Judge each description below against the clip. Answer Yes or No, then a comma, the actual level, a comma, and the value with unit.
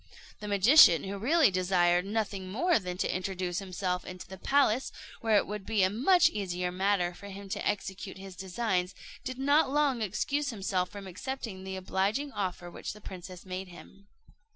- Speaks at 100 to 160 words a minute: No, average, 175 wpm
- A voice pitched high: Yes, high, 195 Hz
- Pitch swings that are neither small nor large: Yes, average, 3.4 semitones